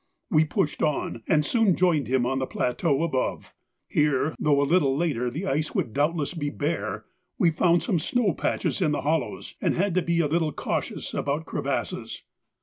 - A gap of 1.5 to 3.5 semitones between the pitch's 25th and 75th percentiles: Yes, average, 3.2 semitones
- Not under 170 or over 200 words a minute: Yes, average, 185 wpm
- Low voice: No, medium, 150 Hz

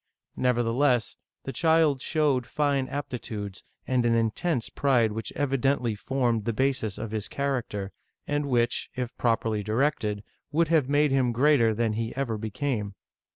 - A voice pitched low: Yes, low, 125 Hz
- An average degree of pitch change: Yes, average, 3.9 semitones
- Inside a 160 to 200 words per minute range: No, average, 150 wpm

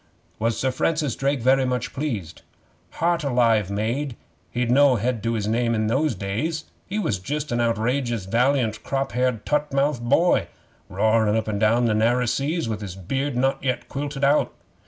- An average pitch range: Yes, average, 4.0 semitones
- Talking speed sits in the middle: Yes, average, 175 wpm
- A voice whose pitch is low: Yes, low, 125 Hz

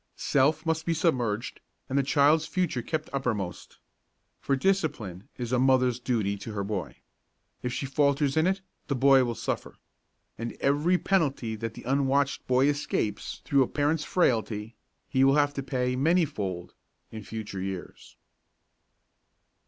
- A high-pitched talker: No, low, 135 Hz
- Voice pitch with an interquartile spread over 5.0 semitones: No, average, 4.4 semitones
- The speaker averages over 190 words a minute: No, average, 155 wpm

